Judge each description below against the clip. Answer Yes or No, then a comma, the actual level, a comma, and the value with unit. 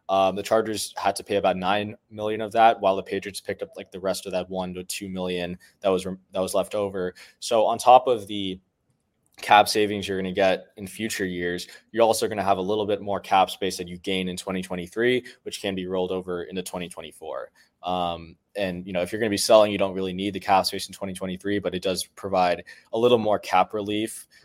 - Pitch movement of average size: No, narrow, 1.9 semitones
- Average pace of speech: No, fast, 240 wpm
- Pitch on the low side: Yes, very low, 95 Hz